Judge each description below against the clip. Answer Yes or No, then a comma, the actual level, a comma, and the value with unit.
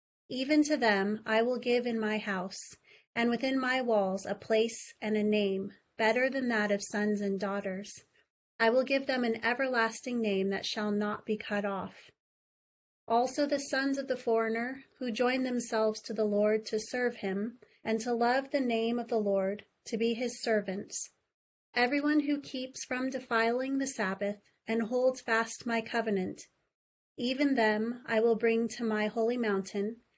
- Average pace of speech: Yes, average, 170 wpm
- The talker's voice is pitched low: No, high, 230 Hz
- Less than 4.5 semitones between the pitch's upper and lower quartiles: Yes, average, 2.9 semitones